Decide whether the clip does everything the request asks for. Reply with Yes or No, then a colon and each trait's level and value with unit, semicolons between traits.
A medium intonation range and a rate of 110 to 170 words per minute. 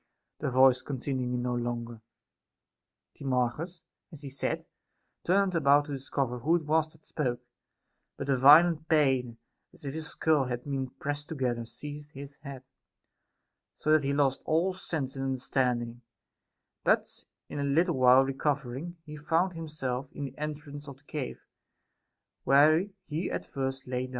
Yes: average, 3.1 semitones; average, 155 wpm